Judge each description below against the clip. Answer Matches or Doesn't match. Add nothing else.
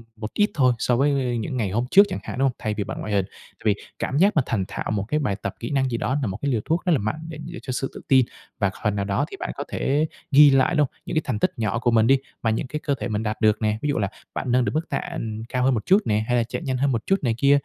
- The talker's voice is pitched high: Doesn't match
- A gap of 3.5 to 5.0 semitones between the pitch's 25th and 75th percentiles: Matches